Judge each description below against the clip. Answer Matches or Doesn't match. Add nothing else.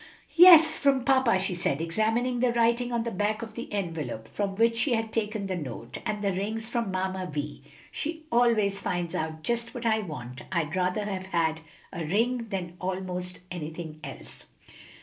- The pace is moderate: Matches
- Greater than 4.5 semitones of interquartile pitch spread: Matches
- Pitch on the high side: Matches